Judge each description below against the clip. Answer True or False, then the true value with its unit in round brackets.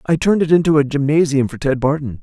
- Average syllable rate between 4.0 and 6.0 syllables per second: False (6.6 syllables/s)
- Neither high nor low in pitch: True (145 Hz)